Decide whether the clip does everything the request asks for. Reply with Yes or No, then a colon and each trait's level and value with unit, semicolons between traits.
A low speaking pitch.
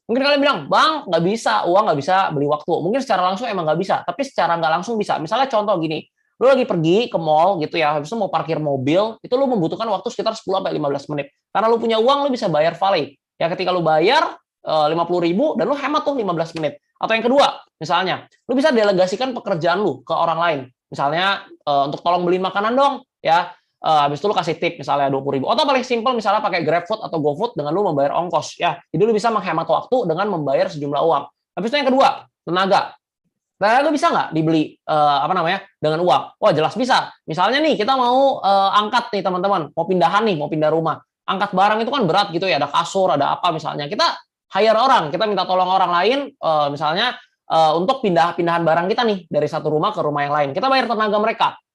No: high, 190 Hz